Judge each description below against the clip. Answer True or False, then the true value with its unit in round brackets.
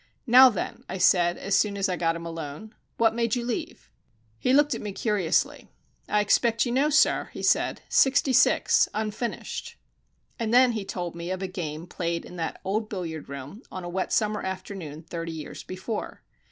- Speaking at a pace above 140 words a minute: True (195 wpm)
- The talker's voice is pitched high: True (195 Hz)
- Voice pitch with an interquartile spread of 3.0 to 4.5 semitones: False (5.0 semitones)